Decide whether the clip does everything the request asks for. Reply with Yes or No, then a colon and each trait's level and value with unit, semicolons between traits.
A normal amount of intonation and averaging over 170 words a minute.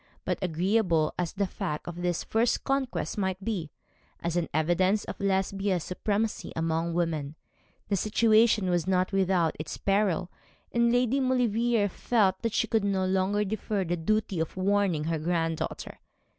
No: average, 3.8 semitones; average, 155 wpm